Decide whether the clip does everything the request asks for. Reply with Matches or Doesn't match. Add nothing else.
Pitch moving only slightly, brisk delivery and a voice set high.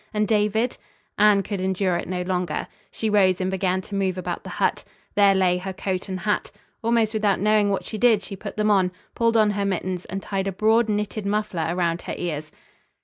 Matches